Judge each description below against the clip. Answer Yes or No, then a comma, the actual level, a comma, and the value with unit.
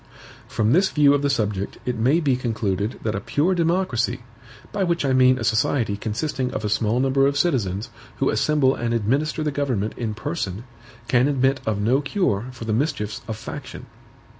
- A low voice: Yes, low, 125 Hz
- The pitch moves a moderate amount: Yes, average, 4.8 semitones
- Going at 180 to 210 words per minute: Yes, average, 190 wpm